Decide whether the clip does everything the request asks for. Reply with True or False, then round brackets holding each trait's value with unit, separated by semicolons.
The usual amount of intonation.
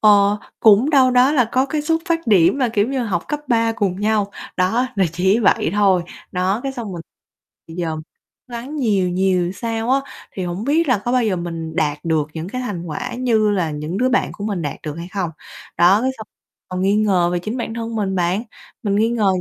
True (5.0 semitones)